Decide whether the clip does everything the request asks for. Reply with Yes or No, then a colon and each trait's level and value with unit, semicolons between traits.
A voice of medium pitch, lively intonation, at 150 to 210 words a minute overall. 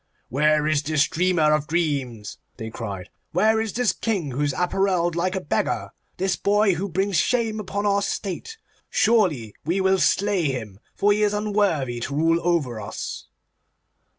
Yes: medium, 175 Hz; wide, 5.7 semitones; average, 160 wpm